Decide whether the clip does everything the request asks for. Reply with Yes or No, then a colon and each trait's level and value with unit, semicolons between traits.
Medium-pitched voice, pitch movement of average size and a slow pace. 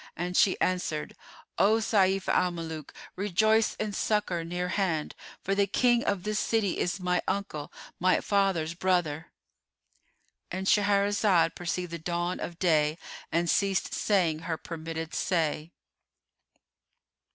Yes: medium, 180 Hz; average, 3.2 semitones; slow, 125 wpm